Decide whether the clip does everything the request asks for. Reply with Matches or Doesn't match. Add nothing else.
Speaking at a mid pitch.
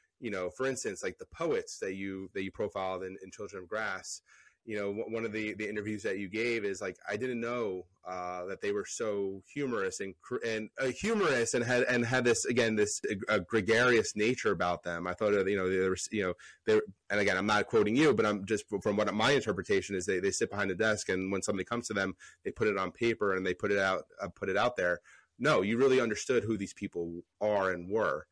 Doesn't match